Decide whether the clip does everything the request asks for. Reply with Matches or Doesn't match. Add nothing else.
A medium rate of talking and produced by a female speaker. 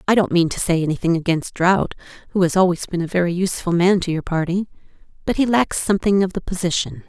Doesn't match